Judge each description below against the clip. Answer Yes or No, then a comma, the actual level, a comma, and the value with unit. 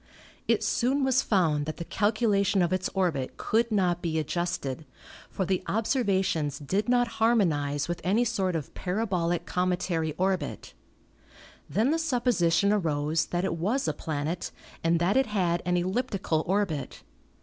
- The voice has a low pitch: No, medium, 185 Hz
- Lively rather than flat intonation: No, average, 4.4 semitones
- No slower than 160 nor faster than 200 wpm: No, average, 150 wpm